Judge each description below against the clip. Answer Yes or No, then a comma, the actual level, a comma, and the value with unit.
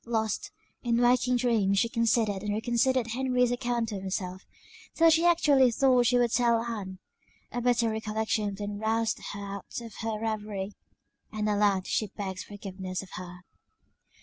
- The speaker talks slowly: No, average, 155 wpm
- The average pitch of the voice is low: No, high, 220 Hz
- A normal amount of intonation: Yes, average, 3.0 semitones